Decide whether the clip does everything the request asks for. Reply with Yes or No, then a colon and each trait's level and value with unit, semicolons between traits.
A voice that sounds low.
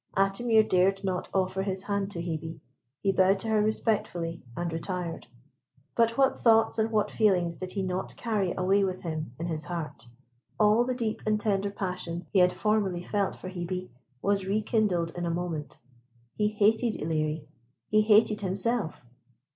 No: high, 190 Hz